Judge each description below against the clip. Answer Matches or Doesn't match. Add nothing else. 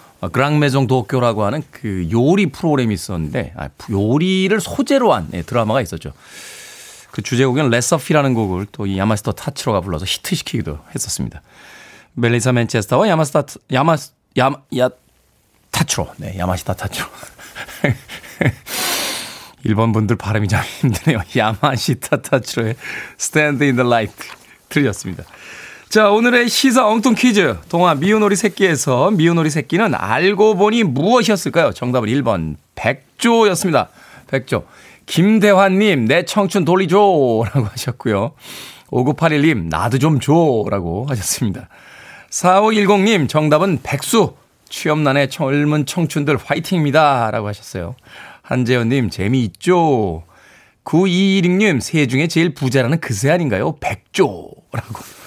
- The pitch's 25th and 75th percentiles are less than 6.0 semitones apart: Doesn't match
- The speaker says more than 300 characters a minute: Doesn't match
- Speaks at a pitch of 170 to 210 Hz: Doesn't match